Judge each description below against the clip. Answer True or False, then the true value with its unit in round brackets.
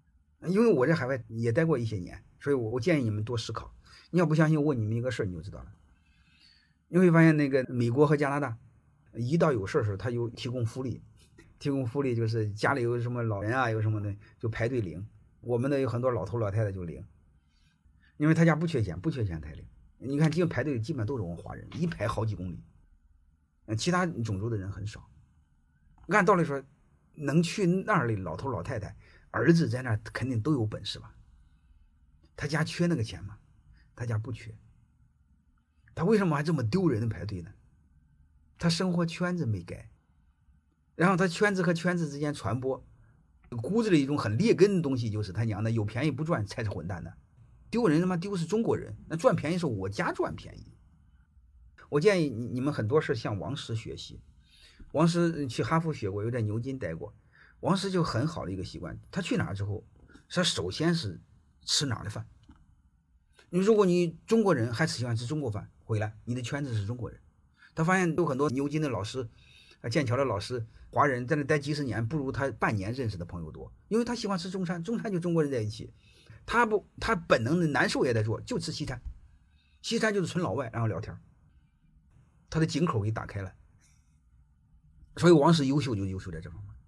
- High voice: False (120 Hz)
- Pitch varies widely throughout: True (8.2 semitones)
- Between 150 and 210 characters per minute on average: False (295 characters per minute)